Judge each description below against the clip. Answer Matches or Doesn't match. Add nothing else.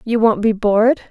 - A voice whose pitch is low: Doesn't match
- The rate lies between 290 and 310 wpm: Doesn't match